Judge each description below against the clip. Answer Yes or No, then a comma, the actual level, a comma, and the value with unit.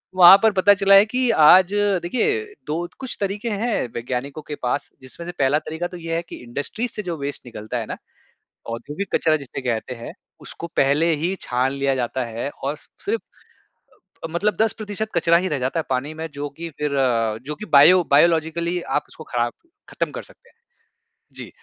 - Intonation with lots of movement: Yes, wide, 5.9 semitones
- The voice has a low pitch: No, medium, 160 Hz